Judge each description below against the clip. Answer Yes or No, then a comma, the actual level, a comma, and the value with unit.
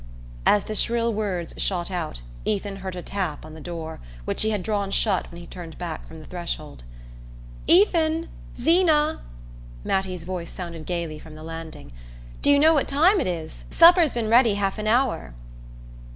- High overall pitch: Yes, high, 195 Hz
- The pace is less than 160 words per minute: No, average, 175 wpm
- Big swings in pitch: Yes, wide, 6.1 semitones